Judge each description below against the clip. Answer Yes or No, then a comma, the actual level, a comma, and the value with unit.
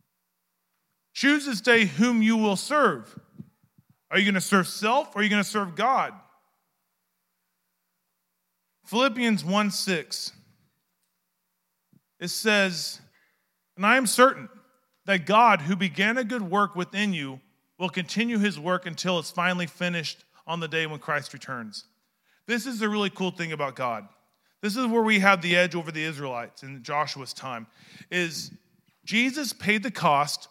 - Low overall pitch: No, medium, 185 Hz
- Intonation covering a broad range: Yes, wide, 6.4 semitones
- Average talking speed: Yes, average, 150 wpm